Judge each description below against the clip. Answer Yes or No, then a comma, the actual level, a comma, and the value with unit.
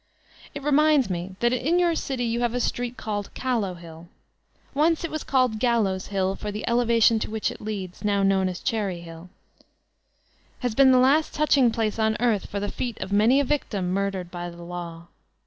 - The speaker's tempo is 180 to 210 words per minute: Yes, average, 200 wpm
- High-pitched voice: Yes, high, 220 Hz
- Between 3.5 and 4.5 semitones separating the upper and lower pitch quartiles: No, average, 5.0 semitones